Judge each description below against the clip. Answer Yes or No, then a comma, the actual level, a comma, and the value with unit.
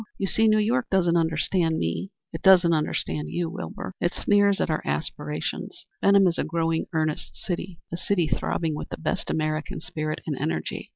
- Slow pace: No, average, 180 wpm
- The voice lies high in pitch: No, medium, 170 Hz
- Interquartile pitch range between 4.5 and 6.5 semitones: No, average, 3.6 semitones